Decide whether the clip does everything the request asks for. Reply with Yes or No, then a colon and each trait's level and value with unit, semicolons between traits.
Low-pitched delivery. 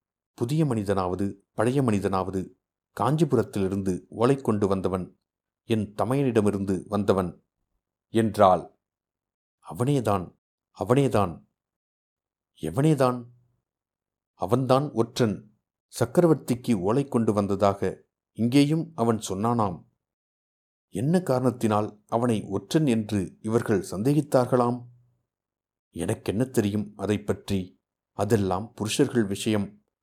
Yes: low, 110 Hz